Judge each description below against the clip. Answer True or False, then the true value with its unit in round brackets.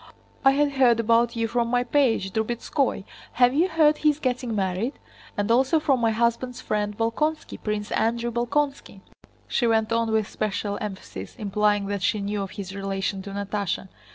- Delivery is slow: False (175 wpm)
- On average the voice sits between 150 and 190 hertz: False (230 Hz)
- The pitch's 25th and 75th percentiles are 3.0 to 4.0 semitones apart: True (3.5 semitones)